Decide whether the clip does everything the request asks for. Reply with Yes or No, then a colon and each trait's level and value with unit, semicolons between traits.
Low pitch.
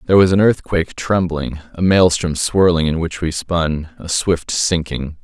Yes: very low, 85 Hz